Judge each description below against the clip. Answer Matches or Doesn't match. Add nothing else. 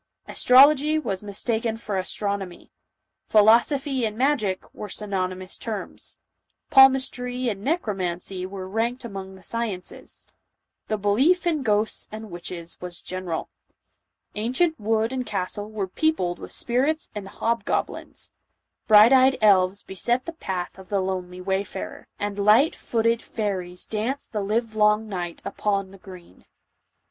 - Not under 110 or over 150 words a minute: Matches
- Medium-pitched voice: Doesn't match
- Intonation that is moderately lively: Matches